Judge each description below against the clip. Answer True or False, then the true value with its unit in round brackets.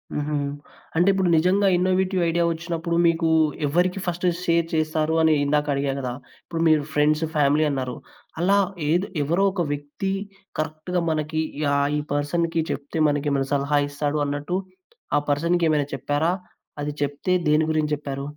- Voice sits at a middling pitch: True (155 Hz)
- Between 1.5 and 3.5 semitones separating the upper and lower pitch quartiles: True (2.9 semitones)